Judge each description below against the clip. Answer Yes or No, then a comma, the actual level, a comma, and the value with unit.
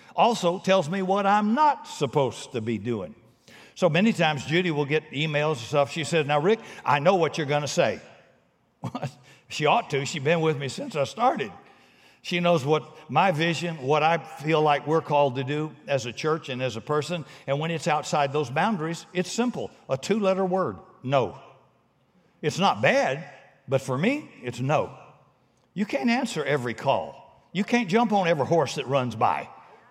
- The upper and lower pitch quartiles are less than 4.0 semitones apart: No, average, 4.5 semitones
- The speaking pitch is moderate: Yes, medium, 155 Hz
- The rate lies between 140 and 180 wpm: No, average, 190 wpm